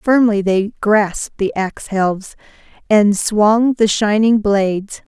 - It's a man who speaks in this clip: No, female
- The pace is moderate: No, slow, 130 wpm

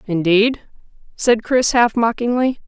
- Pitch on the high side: Yes, high, 230 Hz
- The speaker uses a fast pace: No, slow, 110 wpm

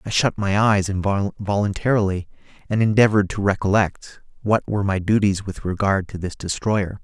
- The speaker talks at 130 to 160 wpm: Yes, average, 155 wpm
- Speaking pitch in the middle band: No, low, 100 Hz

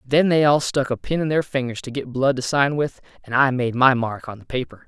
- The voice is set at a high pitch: No, low, 135 Hz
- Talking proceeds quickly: Yes, fast, 285 wpm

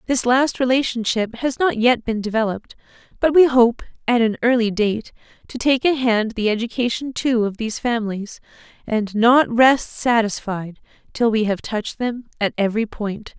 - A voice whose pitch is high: Yes, high, 230 Hz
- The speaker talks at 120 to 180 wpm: Yes, average, 165 wpm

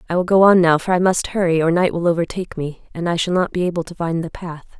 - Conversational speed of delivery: No, fast, 300 wpm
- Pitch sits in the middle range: Yes, medium, 175 Hz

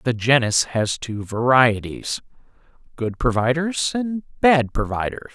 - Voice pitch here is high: No, low, 125 Hz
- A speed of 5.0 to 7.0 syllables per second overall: No, 3.8 syllables/s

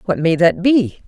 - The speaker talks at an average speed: No, fast, 225 wpm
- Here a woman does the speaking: Yes, female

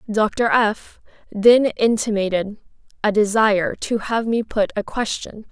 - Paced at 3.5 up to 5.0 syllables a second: Yes, 4.0 syllables/s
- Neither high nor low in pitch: No, high, 215 Hz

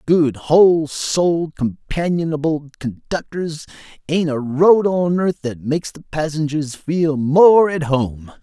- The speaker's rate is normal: No, slow, 130 wpm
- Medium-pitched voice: Yes, medium, 155 Hz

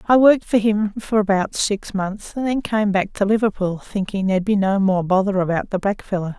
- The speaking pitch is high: Yes, high, 200 Hz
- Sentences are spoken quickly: Yes, fast, 215 wpm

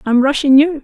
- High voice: Yes, very high, 280 Hz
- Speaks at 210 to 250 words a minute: Yes, fast, 215 wpm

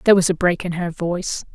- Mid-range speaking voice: Yes, medium, 175 Hz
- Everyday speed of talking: No, fast, 270 wpm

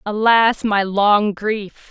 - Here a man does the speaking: No, female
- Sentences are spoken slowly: Yes, slow, 125 wpm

